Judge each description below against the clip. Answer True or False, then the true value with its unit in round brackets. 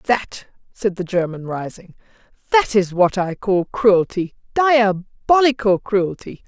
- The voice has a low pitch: False (205 Hz)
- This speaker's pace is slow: True (110 wpm)